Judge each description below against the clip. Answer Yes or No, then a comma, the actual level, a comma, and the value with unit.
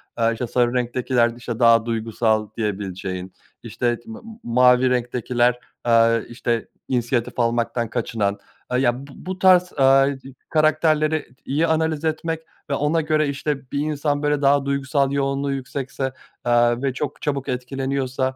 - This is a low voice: Yes, low, 130 Hz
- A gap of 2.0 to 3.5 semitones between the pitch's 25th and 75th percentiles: Yes, average, 3.2 semitones